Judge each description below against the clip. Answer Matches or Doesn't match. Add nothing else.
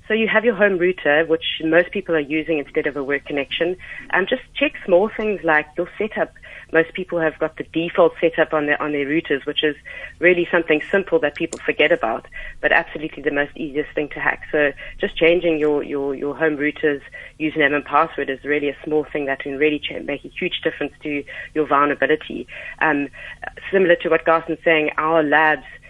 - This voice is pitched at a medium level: Matches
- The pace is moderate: Doesn't match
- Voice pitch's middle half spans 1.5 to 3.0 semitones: Matches